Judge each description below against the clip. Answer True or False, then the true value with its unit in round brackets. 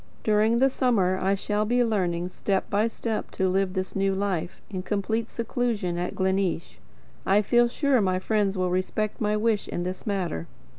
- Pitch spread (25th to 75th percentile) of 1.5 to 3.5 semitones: True (2.9 semitones)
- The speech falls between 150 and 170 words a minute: False (180 wpm)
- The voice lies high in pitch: True (200 Hz)